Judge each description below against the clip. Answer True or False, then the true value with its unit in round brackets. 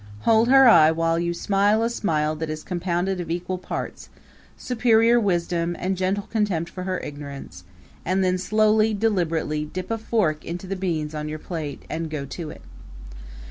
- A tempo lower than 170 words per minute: False (175 wpm)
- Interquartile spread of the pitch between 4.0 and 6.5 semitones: True (4.4 semitones)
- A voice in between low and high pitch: True (180 Hz)